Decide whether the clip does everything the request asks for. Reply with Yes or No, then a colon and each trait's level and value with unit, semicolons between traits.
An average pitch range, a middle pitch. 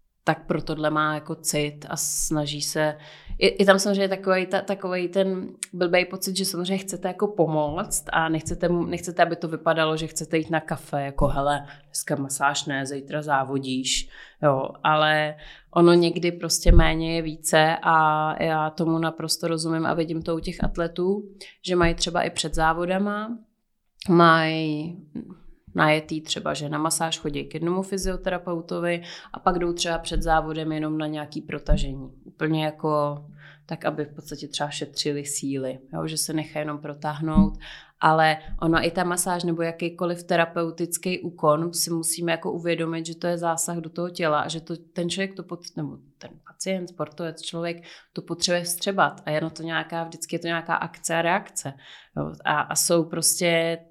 No: narrow, 2.2 semitones; medium, 165 Hz